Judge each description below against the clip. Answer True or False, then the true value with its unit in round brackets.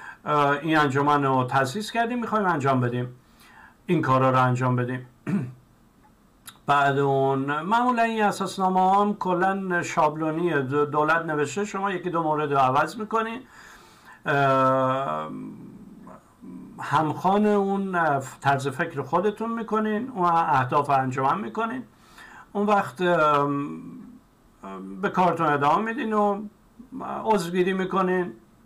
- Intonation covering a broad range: True (6.4 semitones)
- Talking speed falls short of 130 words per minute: True (105 wpm)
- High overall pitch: False (165 Hz)